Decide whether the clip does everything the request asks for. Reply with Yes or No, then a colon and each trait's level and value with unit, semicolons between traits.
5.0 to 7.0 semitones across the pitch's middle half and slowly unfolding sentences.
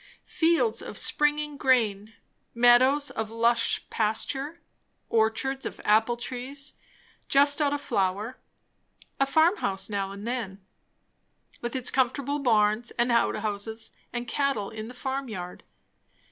No: average, 4.2 semitones; slow, 120 wpm